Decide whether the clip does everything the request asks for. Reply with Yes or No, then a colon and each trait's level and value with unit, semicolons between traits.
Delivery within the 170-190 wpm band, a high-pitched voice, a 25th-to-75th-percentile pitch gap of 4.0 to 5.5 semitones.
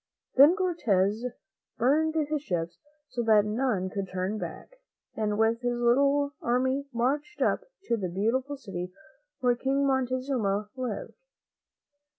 No: slow, 135 wpm; high, 245 Hz; average, 4.8 semitones